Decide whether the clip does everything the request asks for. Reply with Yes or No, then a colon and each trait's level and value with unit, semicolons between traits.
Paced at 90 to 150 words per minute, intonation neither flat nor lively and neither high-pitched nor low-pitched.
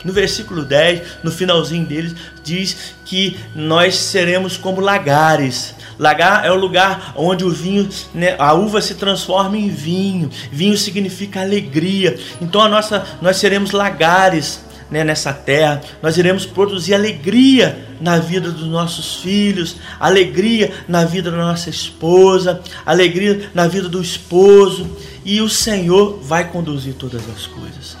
Yes: average, 140 wpm; average, 3.4 semitones; medium, 180 Hz